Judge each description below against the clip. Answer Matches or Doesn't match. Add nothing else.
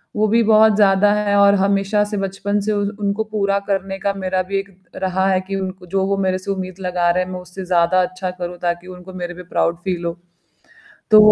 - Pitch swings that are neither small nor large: Doesn't match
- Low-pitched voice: Doesn't match